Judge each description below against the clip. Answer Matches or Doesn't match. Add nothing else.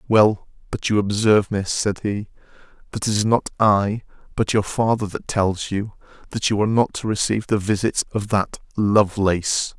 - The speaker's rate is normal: Matches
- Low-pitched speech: Matches